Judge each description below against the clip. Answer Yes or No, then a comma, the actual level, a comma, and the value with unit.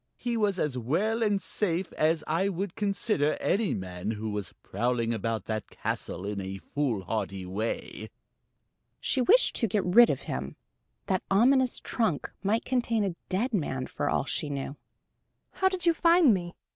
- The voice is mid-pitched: Yes, medium, 175 Hz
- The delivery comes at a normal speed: Yes, average, 165 wpm